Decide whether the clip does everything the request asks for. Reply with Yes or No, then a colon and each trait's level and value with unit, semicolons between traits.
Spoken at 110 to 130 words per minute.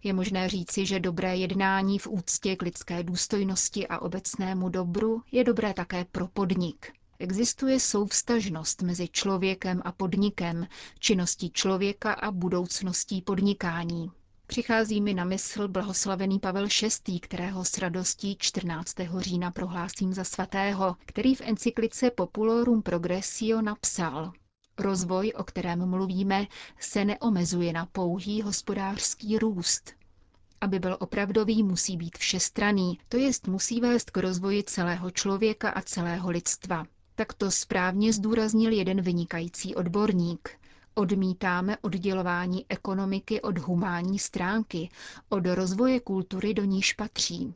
Yes: average, 120 wpm